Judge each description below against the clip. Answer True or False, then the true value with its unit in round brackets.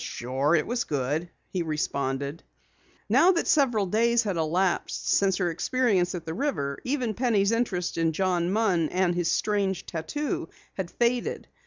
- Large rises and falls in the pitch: True (5.9 semitones)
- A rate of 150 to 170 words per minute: True (155 wpm)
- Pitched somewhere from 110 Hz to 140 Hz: False (185 Hz)